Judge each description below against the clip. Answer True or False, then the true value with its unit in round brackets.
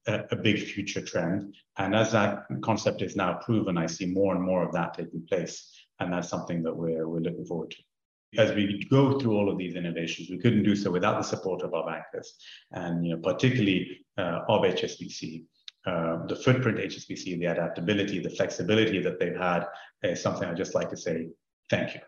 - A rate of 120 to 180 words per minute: False (205 wpm)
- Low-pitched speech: True (95 Hz)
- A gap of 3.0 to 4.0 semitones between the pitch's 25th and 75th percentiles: True (3.6 semitones)